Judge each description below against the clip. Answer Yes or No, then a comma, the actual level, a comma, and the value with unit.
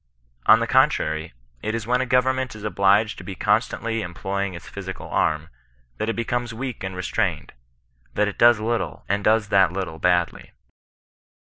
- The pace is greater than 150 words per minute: Yes, average, 185 wpm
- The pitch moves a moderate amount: Yes, average, 4.0 semitones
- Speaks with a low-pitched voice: Yes, low, 105 Hz